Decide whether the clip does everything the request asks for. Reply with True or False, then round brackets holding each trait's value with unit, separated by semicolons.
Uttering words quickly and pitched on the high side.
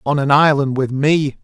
False (210 wpm; 140 Hz)